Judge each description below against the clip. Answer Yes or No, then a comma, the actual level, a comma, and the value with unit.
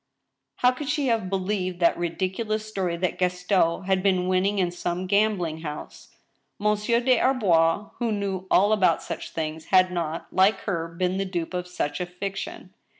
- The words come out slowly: No, average, 170 wpm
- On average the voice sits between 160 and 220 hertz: Yes, medium, 185 Hz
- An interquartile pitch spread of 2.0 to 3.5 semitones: Yes, average, 2.9 semitones